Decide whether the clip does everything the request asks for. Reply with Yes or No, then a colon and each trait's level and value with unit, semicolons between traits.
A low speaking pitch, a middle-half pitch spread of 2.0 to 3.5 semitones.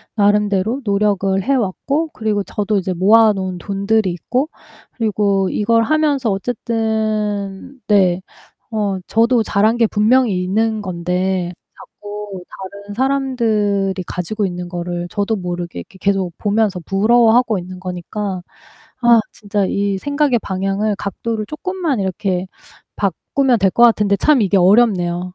No: high, 205 Hz; average, 3.1 semitones